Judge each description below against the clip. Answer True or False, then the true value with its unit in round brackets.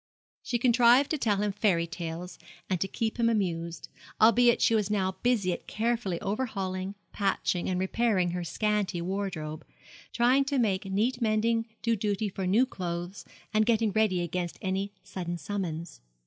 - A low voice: False (200 Hz)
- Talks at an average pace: True (160 wpm)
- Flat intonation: False (4.0 semitones)